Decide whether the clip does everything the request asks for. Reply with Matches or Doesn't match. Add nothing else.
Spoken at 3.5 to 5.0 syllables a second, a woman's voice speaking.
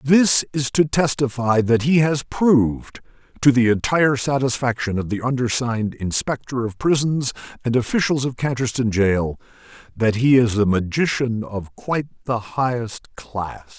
Doesn't match